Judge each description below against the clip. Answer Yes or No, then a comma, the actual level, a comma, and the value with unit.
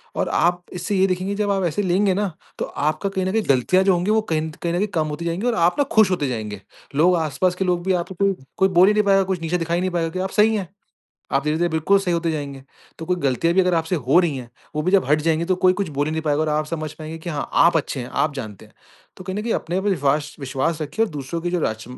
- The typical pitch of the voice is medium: Yes, medium, 170 Hz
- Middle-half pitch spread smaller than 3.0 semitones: No, average, 3.7 semitones